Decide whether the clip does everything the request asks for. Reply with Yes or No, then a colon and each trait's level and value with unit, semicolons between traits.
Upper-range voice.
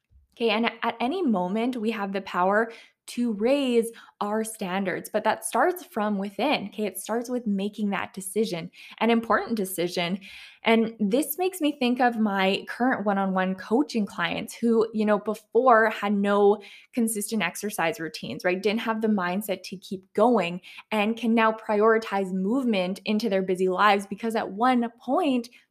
Yes: high, 215 Hz